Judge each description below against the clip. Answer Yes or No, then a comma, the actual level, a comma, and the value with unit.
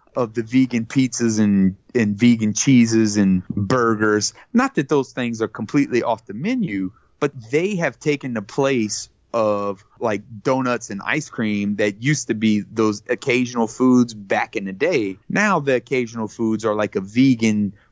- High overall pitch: No, low, 115 Hz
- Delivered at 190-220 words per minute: No, average, 165 wpm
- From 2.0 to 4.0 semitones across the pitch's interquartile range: Yes, average, 3.6 semitones